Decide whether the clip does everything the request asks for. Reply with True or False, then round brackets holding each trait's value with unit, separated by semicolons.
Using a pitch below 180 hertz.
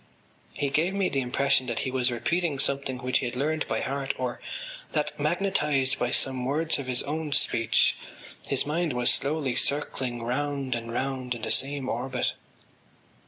True (135 Hz)